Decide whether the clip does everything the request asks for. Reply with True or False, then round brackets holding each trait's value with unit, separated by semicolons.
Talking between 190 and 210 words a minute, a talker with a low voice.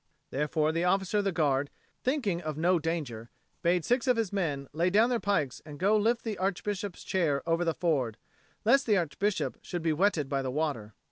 False (200 wpm; 170 Hz)